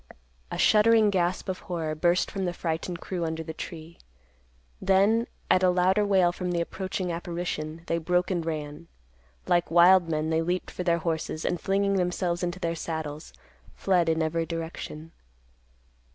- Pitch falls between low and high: Yes, medium, 175 Hz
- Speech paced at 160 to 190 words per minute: Yes, average, 165 wpm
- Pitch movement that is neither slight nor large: No, narrow, 2.2 semitones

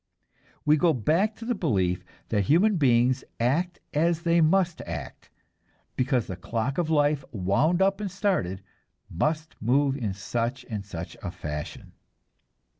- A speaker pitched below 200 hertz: Yes, medium, 140 Hz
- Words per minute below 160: Yes, average, 145 wpm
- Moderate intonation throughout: No, wide, 7.8 semitones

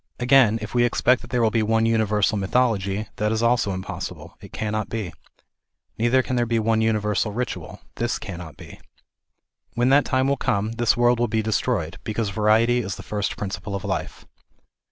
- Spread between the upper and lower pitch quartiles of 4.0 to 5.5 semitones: No, narrow, 2.6 semitones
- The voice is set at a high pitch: No, low, 110 Hz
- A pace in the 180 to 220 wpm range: Yes, average, 185 wpm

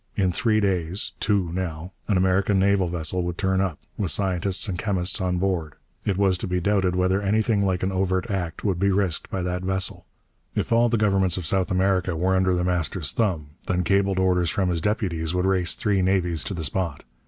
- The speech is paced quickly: Yes, fast, 210 wpm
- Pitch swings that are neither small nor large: No, narrow, 1.7 semitones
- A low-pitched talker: Yes, very low, 95 Hz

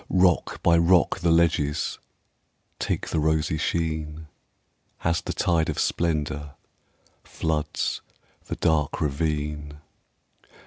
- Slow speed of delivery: Yes, slow, 100 wpm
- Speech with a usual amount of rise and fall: No, narrow, 1.8 semitones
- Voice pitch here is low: Yes, very low, 80 Hz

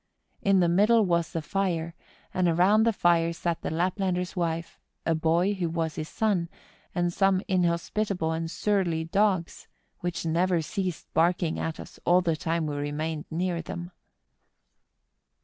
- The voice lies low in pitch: No, medium, 175 Hz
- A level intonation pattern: Yes, narrow, 2.2 semitones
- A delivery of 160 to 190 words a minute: No, average, 150 wpm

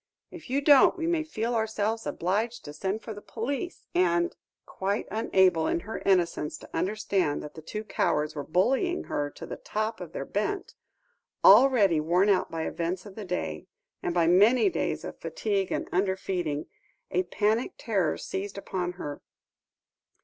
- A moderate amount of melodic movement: Yes, average, 4.3 semitones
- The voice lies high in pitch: Yes, high, 195 Hz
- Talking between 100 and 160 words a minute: No, average, 175 wpm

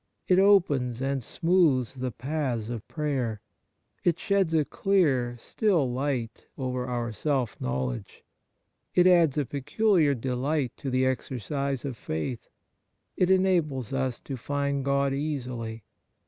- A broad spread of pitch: No, average, 3.9 semitones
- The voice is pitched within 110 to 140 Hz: Yes, low, 135 Hz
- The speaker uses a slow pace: Yes, slow, 130 wpm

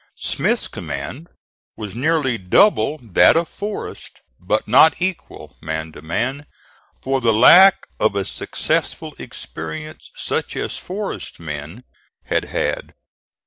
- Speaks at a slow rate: Yes, slow, 120 wpm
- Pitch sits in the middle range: No, low, 120 Hz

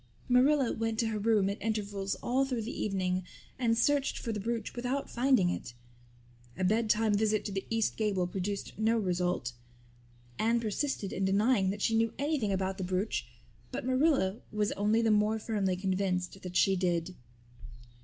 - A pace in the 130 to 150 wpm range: No, average, 170 wpm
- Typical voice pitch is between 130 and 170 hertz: No, high, 210 Hz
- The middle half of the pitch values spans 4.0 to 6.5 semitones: No, average, 3.1 semitones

